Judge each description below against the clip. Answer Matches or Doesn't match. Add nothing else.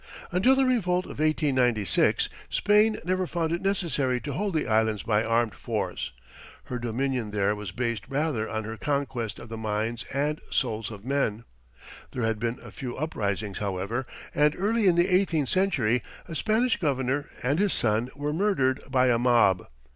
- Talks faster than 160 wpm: Matches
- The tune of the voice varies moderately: Doesn't match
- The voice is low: Matches